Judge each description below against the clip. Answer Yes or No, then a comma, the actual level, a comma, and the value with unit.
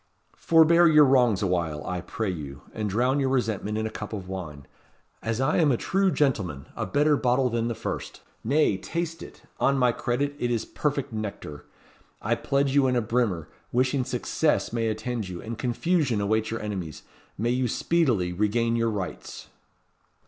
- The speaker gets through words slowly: No, average, 180 wpm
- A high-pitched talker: No, low, 115 Hz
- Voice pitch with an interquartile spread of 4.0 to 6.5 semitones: Yes, average, 4.8 semitones